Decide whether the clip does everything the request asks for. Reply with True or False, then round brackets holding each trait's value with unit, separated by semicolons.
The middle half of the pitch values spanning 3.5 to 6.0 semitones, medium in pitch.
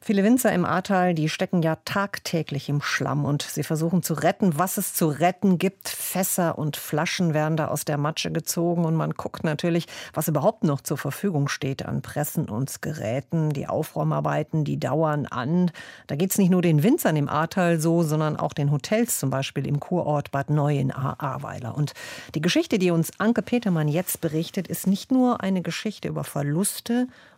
True (4.1 semitones; 165 Hz)